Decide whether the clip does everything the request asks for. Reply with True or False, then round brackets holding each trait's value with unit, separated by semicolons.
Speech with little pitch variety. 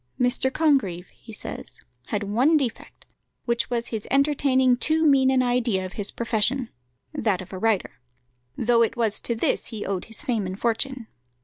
False (3.8 semitones)